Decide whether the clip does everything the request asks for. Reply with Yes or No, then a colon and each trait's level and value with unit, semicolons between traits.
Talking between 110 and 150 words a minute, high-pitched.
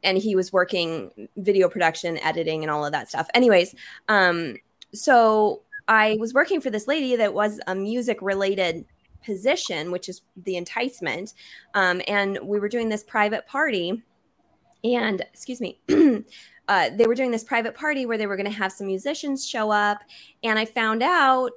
No: average, 175 wpm; high, 210 Hz